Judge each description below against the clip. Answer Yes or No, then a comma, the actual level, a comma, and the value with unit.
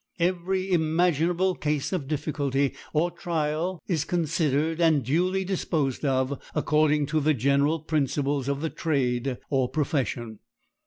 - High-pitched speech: No, medium, 150 Hz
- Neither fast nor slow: No, slow, 125 wpm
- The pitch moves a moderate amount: Yes, average, 3.4 semitones